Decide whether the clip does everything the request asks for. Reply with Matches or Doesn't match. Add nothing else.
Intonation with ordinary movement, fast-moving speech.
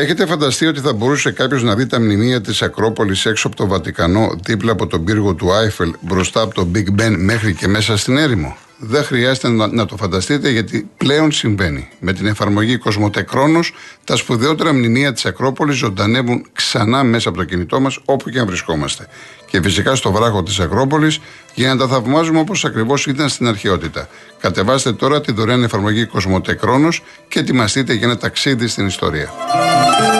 Matches